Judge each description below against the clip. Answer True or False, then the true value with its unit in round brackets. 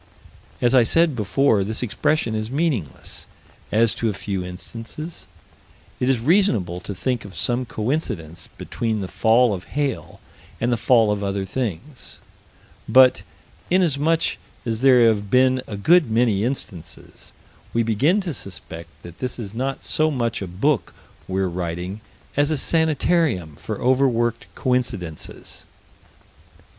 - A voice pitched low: True (115 Hz)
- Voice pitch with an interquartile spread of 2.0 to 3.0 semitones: False (5.3 semitones)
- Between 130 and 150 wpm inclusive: True (140 wpm)